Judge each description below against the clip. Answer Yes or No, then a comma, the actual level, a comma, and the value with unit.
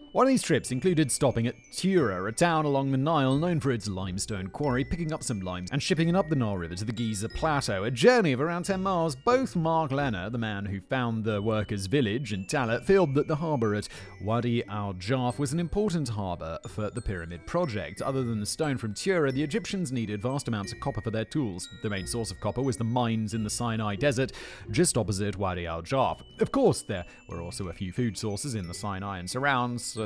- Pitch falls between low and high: No, low, 120 Hz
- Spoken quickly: Yes, fast, 225 wpm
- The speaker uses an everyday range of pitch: No, wide, 6.1 semitones